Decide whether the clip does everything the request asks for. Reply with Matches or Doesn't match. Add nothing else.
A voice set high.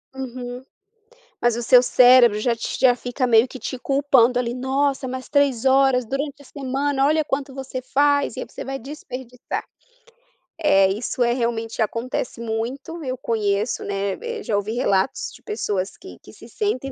Matches